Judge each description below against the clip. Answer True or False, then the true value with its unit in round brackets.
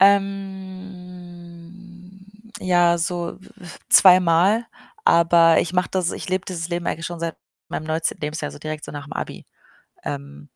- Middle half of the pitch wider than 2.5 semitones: False (2.2 semitones)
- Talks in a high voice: False (175 Hz)